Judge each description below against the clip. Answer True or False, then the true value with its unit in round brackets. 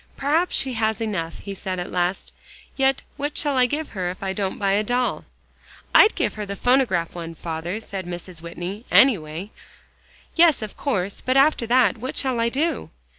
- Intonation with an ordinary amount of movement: False (6.3 semitones)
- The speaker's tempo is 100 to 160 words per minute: False (185 wpm)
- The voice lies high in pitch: True (215 Hz)